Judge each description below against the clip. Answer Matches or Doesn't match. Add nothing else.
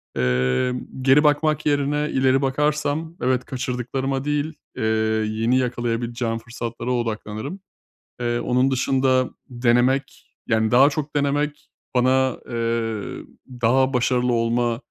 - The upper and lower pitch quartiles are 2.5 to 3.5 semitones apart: Matches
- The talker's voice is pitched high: Doesn't match